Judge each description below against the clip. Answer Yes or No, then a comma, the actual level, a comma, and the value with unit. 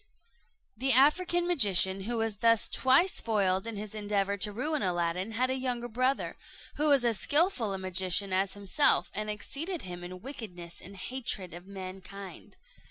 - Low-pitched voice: No, high, 210 Hz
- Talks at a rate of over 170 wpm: No, average, 165 wpm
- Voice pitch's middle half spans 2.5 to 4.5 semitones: No, wide, 5.4 semitones